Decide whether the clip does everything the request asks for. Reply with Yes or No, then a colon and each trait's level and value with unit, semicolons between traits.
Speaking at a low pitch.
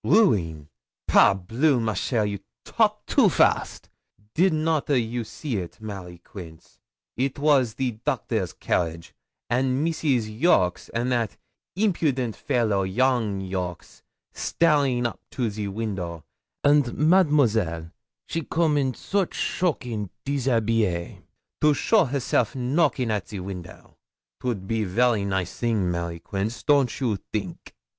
Yes: low, 115 Hz